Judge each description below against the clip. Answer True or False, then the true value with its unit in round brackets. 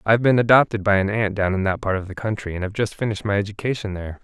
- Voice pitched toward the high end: False (105 Hz)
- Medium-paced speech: False (295 wpm)